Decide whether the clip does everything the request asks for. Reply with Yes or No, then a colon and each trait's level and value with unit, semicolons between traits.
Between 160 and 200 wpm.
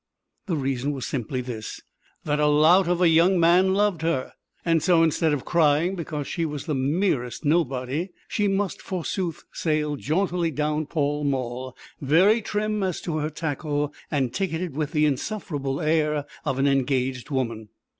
Yes: average, 165 wpm